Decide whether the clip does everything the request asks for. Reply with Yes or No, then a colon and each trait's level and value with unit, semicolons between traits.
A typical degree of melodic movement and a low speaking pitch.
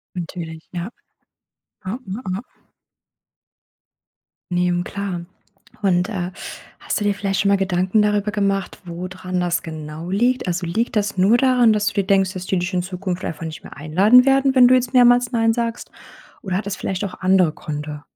No: average, 3.2 semitones; high, 190 Hz